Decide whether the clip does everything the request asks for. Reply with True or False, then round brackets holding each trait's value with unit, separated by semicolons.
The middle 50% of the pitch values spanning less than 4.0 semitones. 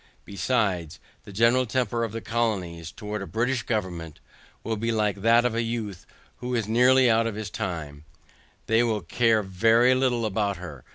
True (3.4 semitones)